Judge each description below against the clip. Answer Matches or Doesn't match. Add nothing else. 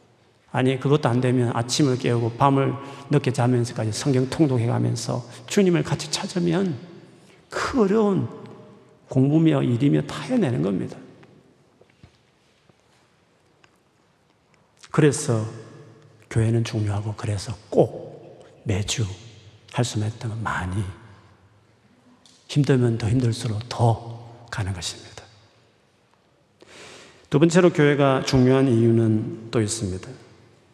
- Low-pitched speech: Matches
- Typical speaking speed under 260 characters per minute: Matches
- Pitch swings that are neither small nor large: Matches